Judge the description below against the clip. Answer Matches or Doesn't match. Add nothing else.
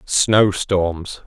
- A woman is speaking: Doesn't match